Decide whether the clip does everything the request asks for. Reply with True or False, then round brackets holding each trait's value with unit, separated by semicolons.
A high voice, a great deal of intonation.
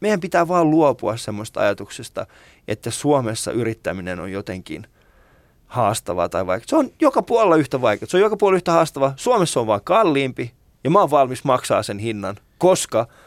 False (135 Hz; 8.6 semitones)